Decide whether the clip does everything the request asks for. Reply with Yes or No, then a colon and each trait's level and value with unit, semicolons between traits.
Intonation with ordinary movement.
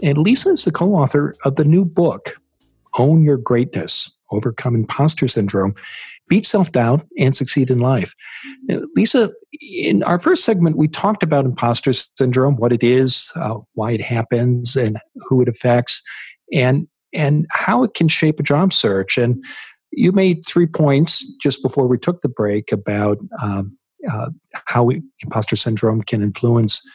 No: wide, 5.9 semitones